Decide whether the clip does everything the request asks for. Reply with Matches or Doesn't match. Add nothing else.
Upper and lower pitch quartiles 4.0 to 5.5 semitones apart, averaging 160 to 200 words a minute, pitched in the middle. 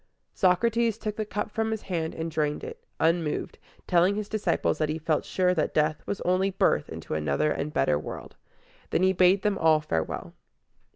Matches